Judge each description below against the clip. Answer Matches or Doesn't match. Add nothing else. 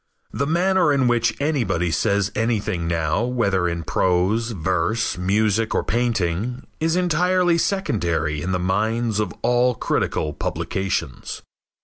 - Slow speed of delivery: Matches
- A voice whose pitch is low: Matches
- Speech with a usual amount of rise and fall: Doesn't match